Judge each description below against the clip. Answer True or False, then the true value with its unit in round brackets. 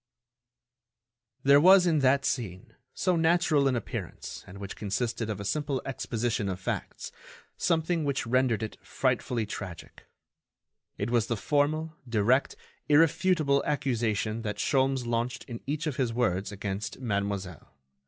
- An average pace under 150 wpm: True (135 wpm)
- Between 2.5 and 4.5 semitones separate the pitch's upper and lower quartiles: False (5.3 semitones)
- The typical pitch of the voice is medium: False (125 Hz)